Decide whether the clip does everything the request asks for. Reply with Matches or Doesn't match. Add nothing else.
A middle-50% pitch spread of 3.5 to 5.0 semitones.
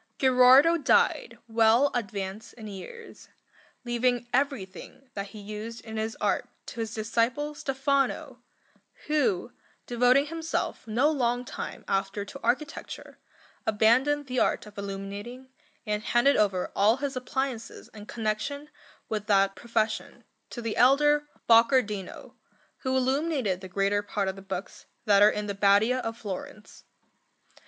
Matches